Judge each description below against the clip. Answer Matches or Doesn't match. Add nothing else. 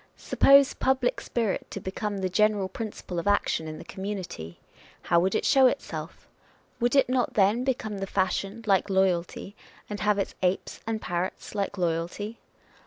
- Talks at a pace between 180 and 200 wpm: Doesn't match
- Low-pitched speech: Doesn't match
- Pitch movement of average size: Matches